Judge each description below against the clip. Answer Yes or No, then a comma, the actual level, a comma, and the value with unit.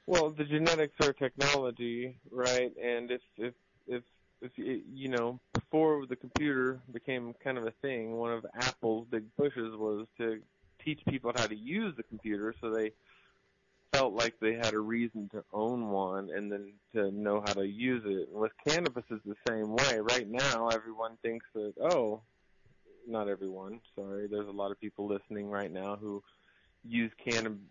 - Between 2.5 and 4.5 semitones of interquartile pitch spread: Yes, average, 3.1 semitones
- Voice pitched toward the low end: Yes, low, 115 Hz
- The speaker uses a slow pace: No, average, 175 wpm